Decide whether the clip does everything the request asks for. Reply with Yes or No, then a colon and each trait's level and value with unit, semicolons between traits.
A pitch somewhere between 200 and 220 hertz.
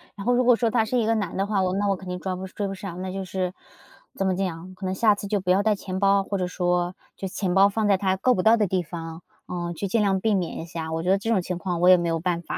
No: high, 190 Hz